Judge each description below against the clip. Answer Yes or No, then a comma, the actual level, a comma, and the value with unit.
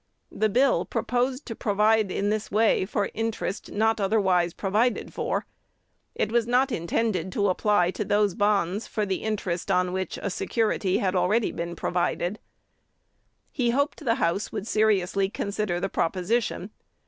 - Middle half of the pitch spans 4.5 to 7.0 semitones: No, average, 3.1 semitones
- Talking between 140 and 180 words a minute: Yes, average, 150 wpm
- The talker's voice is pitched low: No, high, 205 Hz